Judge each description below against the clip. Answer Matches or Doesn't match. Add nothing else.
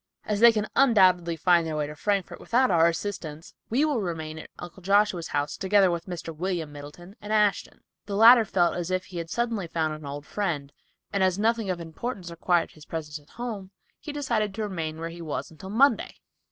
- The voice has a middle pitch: Matches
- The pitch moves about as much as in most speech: Matches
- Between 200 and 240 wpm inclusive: Matches